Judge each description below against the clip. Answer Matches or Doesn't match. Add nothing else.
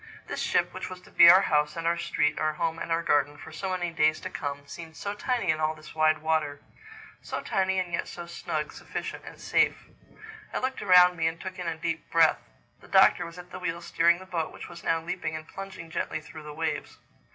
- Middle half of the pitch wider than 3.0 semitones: Doesn't match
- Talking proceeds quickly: Matches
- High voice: Doesn't match